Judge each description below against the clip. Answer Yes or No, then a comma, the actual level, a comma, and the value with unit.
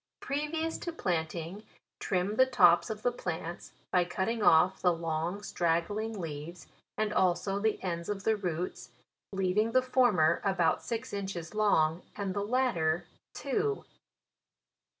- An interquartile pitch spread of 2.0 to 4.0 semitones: No, average, 4.4 semitones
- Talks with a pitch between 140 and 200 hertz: Yes, high, 190 Hz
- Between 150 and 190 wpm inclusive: No, average, 140 wpm